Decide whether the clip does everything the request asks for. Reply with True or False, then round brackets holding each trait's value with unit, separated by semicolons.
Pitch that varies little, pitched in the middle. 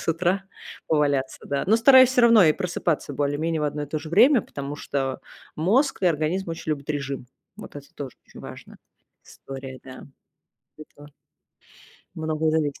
False (4.1 semitones; 155 Hz)